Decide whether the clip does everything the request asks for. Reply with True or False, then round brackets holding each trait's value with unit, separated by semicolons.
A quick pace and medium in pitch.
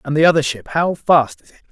True (245 wpm; 155 Hz)